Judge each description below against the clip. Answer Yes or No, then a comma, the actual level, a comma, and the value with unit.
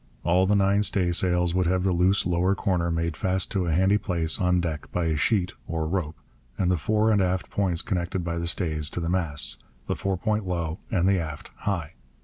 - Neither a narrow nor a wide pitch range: No, narrow, 2.3 semitones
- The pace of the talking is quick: Yes, fast, 215 wpm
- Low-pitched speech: Yes, very low, 90 Hz